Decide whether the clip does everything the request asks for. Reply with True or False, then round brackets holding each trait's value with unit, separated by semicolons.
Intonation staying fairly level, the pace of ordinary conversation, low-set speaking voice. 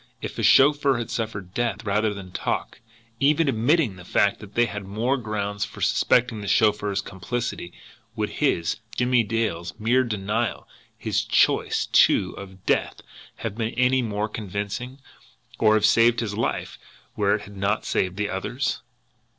False (3.0 semitones; 160 wpm; 110 Hz)